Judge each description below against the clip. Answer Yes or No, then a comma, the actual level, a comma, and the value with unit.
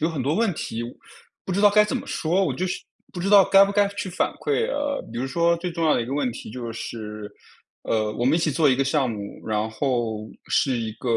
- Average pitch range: No, wide, 8.0 semitones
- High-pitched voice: No, medium, 145 Hz